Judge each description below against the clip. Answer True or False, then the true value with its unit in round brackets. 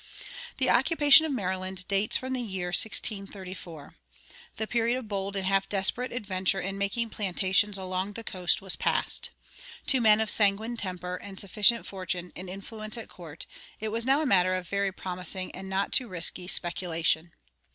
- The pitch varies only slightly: False (3.0 semitones)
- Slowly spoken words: False (170 wpm)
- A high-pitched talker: True (195 Hz)